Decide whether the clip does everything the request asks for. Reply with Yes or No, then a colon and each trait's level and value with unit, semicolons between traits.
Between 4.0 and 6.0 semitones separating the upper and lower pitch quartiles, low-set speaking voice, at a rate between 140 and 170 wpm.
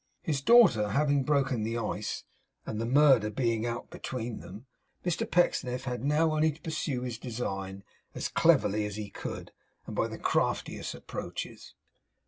Yes: average, 5.0 semitones; low, 125 Hz; average, 155 wpm